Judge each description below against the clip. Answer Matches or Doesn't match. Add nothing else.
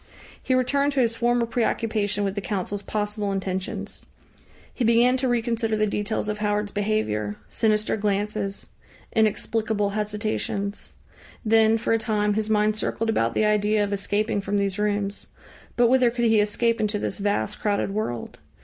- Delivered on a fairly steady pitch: Matches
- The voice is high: Matches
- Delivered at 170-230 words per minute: Doesn't match